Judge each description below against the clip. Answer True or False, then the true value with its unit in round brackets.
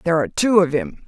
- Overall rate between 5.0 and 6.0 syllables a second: False (8.3 syllables/s)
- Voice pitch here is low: False (175 Hz)